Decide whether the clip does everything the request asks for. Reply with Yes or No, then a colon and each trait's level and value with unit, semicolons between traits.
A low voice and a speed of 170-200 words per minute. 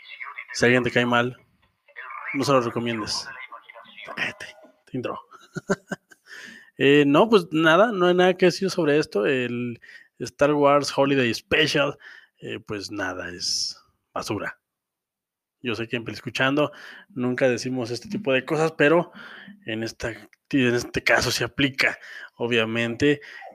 No: low, 130 Hz; average, 140 wpm